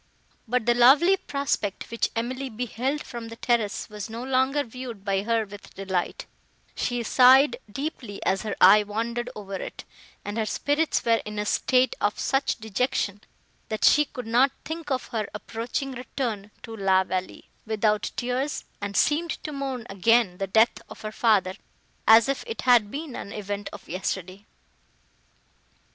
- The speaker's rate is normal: Yes, average, 160 wpm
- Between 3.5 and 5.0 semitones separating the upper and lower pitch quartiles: Yes, average, 4.0 semitones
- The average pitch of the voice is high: Yes, high, 230 Hz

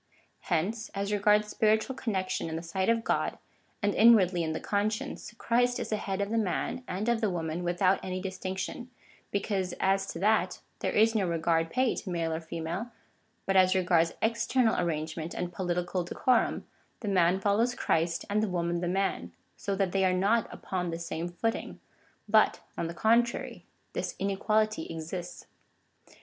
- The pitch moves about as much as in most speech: Yes, average, 3.8 semitones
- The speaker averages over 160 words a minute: Yes, average, 175 wpm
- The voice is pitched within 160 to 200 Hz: Yes, high, 190 Hz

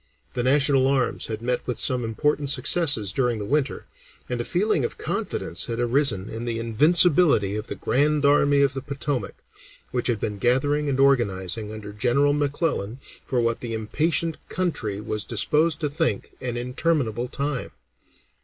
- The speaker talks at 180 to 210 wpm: No, average, 165 wpm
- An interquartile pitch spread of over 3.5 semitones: Yes, average, 4.2 semitones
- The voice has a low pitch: Yes, low, 130 Hz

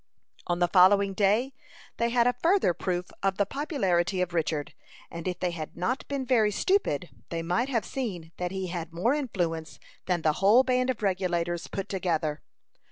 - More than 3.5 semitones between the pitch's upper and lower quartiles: Yes, wide, 5.6 semitones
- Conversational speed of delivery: Yes, average, 180 wpm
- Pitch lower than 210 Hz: Yes, high, 190 Hz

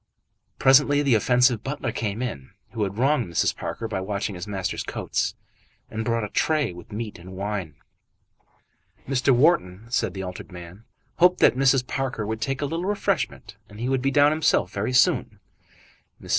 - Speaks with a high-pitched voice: No, low, 115 Hz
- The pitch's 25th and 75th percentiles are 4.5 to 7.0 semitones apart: Yes, average, 5.2 semitones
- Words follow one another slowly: No, average, 175 wpm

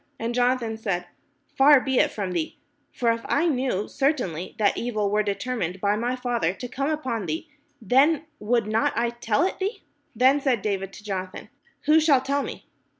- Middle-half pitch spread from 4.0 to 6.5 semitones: Yes, average, 4.6 semitones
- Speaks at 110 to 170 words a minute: No, average, 190 wpm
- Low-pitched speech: No, high, 235 Hz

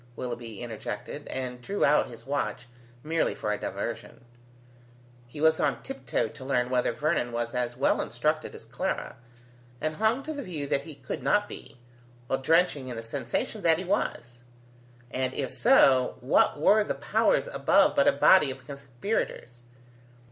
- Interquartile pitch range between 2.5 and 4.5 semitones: No, average, 5.0 semitones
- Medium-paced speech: Yes, average, 165 wpm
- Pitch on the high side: No, low, 135 Hz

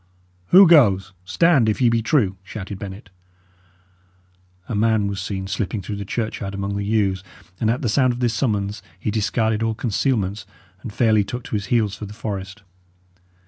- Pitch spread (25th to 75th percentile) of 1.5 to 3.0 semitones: Yes, average, 2.7 semitones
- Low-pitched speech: Yes, low, 105 Hz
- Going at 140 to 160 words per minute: No, average, 180 wpm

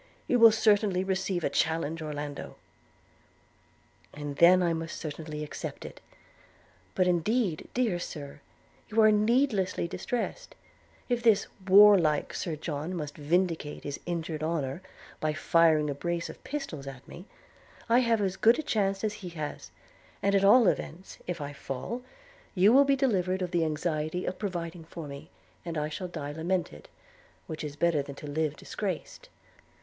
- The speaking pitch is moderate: Yes, medium, 175 Hz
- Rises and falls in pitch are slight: No, average, 4.9 semitones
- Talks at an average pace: Yes, average, 160 wpm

